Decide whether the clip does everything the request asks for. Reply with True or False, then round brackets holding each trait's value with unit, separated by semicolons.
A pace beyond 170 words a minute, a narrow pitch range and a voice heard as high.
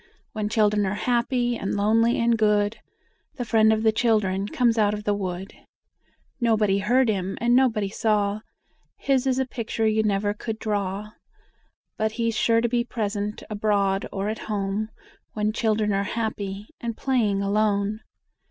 False (160 wpm; 2.0 semitones; 215 Hz)